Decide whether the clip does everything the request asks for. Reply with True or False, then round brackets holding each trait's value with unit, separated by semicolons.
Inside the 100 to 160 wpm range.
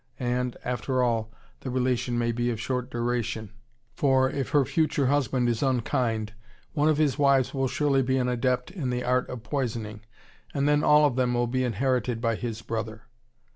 False (185 wpm)